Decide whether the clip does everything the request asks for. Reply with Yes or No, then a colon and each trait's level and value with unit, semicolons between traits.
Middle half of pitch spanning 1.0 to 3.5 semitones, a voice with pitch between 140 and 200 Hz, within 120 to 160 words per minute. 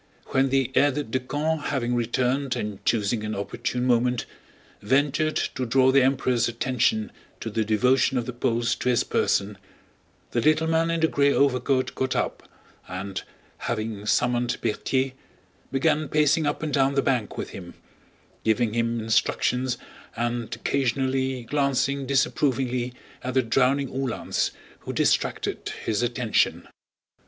No: average, 2.7 semitones; low, 125 Hz; average, 140 wpm